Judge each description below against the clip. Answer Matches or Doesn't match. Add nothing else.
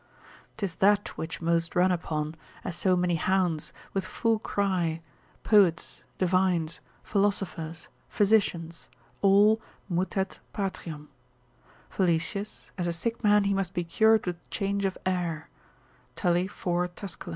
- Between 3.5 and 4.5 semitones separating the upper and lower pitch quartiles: Doesn't match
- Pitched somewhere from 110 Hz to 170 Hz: Doesn't match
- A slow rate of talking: Matches